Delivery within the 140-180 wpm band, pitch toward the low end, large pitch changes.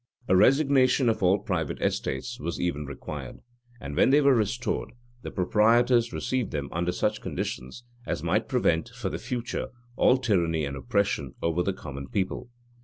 Yes: average, 170 wpm; low, 100 Hz; wide, 6.8 semitones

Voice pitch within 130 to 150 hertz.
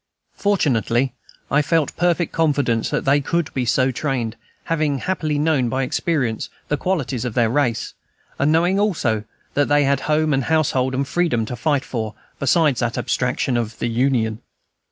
Yes: low, 135 Hz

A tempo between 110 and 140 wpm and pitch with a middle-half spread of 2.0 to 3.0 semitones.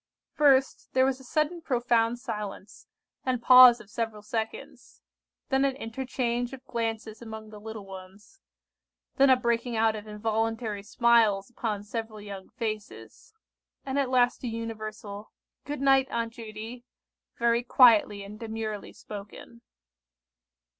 Yes: slow, 135 wpm; average, 2.7 semitones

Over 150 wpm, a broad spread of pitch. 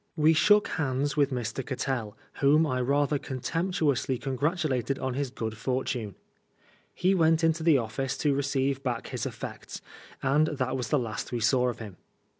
No: average, 165 wpm; average, 3.2 semitones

